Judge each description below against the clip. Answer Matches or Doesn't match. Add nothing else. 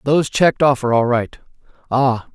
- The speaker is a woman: Doesn't match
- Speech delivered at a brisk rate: Doesn't match